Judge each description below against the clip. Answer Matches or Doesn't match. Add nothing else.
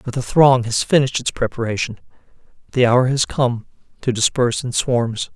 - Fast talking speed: Doesn't match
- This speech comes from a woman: Doesn't match